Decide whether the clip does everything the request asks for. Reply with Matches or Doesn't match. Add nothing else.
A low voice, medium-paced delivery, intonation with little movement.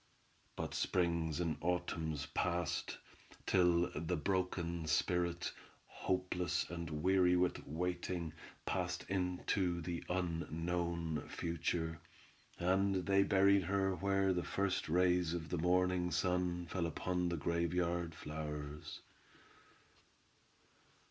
Doesn't match